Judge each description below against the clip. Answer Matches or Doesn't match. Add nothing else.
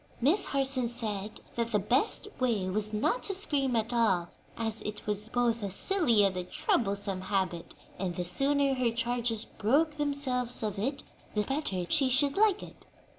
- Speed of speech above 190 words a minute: Doesn't match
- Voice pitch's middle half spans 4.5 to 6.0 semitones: Matches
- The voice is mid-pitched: Doesn't match